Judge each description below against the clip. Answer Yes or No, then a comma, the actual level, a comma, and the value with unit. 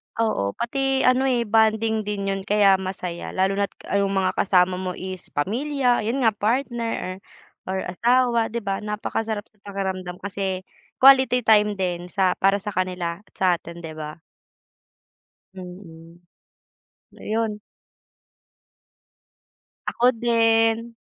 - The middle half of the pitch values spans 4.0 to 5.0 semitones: No, average, 3.5 semitones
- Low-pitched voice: No, high, 205 Hz